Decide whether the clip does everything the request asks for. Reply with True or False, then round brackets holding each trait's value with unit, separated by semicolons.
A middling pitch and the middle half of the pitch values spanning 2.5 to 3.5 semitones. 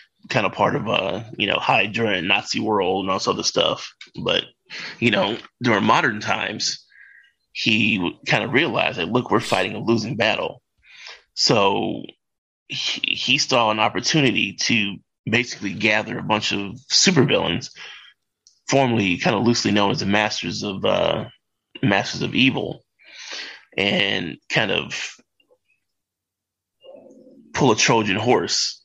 False (105 Hz; 2.8 semitones)